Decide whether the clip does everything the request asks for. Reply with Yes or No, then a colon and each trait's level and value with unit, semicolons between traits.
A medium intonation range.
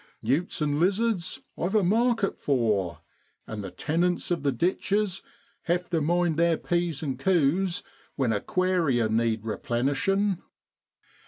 No: wide, 6.1 semitones